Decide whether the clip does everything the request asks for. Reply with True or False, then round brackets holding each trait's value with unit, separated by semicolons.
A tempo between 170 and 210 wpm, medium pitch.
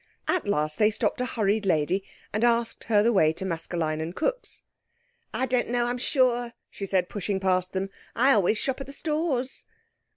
False (190 wpm; 215 Hz)